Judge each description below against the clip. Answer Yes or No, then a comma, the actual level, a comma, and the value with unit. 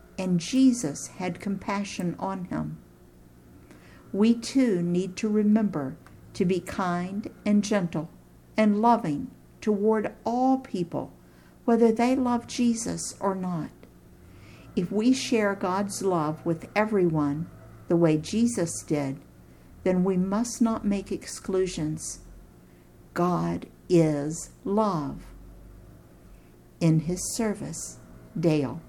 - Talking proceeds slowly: Yes, slow, 105 wpm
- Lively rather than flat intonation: Yes, wide, 6.4 semitones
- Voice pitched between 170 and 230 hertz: Yes, medium, 185 Hz